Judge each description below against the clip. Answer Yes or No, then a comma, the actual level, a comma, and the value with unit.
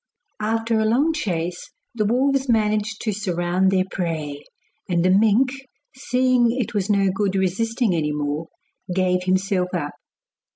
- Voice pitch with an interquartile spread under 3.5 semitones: No, average, 4.0 semitones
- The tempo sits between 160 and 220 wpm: No, average, 140 wpm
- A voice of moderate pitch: No, high, 195 Hz